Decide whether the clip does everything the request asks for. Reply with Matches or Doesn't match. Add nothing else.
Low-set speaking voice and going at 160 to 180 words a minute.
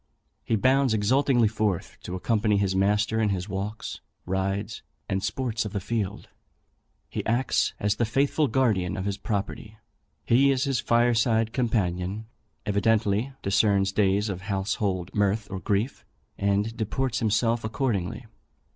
Doesn't match